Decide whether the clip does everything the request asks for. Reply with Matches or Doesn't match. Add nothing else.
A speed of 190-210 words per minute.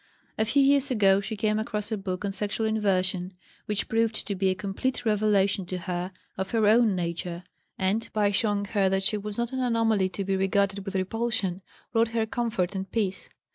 Matches